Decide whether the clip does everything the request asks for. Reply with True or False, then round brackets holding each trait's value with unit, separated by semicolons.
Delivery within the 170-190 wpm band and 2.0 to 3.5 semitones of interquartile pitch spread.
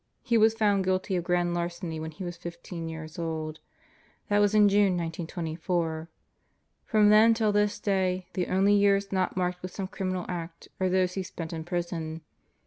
True (180 wpm; 2.9 semitones)